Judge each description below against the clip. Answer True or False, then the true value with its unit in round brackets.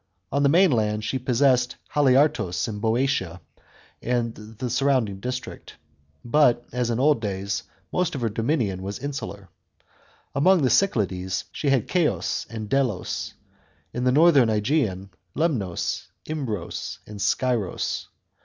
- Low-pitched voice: True (120 Hz)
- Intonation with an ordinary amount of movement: True (4.8 semitones)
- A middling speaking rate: False (125 wpm)